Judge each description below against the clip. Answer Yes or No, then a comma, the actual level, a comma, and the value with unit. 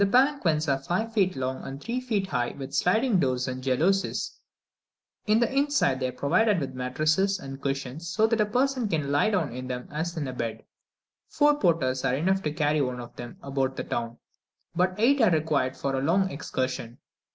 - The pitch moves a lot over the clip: Yes, wide, 7.2 semitones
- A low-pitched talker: No, medium, 155 Hz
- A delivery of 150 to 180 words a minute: No, average, 200 wpm